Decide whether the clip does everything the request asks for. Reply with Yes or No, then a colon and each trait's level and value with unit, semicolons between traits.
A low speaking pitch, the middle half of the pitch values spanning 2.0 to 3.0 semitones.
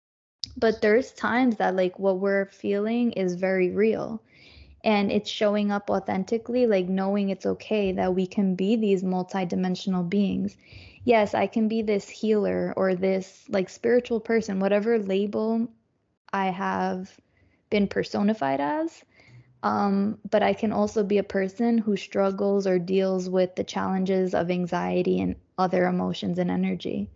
No: high, 195 Hz; narrow, 2.5 semitones